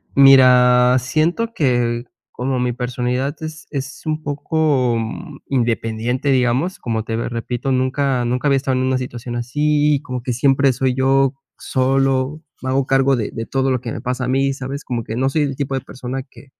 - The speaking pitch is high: No, low, 130 Hz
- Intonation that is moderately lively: No, narrow, 1.9 semitones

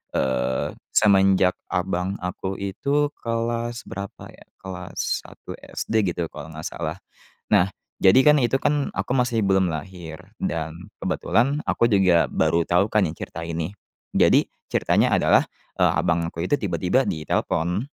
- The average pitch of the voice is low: Yes, very low, 95 Hz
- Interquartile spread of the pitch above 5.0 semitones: Yes, wide, 5.4 semitones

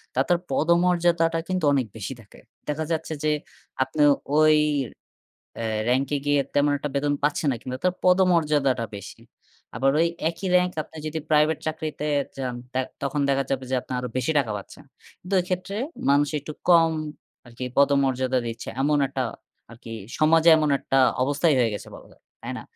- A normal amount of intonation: Yes, average, 3.7 semitones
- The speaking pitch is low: No, medium, 145 Hz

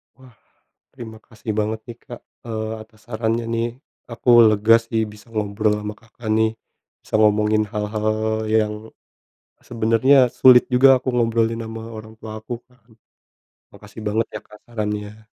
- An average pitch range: No, narrow, 1.4 semitones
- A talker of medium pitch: No, low, 110 Hz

